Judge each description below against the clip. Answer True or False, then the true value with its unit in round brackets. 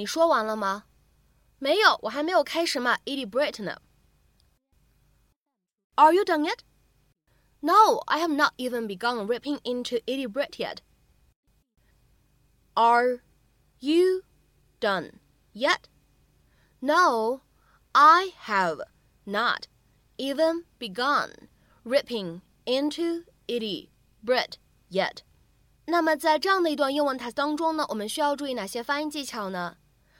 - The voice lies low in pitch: False (280 Hz)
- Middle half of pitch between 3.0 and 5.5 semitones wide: True (5.2 semitones)